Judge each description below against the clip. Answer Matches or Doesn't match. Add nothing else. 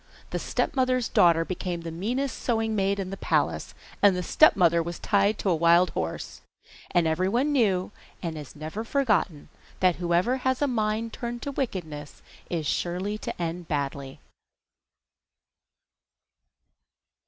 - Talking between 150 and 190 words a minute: Doesn't match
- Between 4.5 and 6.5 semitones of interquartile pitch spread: Matches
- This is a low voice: Doesn't match